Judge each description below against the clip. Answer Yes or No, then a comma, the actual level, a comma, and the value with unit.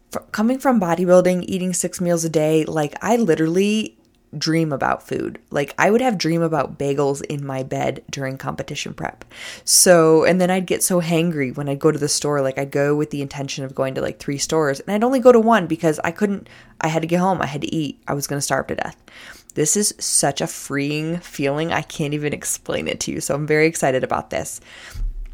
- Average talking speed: No, fast, 225 wpm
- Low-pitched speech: No, medium, 160 Hz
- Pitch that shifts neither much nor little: Yes, average, 4.2 semitones